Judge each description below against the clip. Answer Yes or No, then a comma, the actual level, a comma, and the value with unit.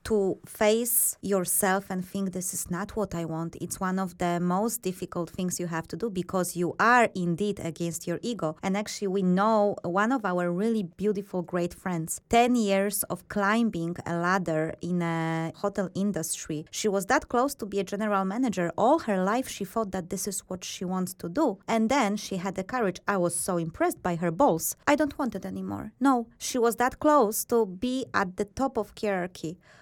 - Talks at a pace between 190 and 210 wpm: Yes, fast, 205 wpm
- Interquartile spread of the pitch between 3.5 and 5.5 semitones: Yes, average, 3.8 semitones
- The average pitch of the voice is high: Yes, high, 195 Hz